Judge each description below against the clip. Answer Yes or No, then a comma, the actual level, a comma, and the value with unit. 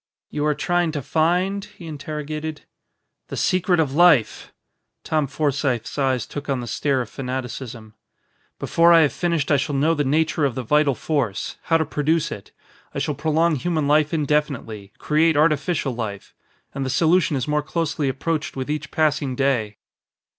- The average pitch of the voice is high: No, medium, 150 Hz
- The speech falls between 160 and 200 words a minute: Yes, average, 170 wpm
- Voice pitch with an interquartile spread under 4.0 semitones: Yes, average, 3.0 semitones